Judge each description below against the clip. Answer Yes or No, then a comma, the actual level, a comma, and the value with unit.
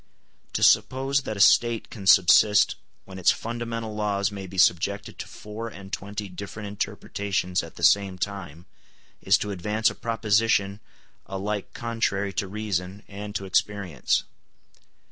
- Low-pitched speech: Yes, low, 100 Hz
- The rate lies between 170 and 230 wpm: No, average, 145 wpm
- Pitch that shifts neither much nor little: No, narrow, 1.9 semitones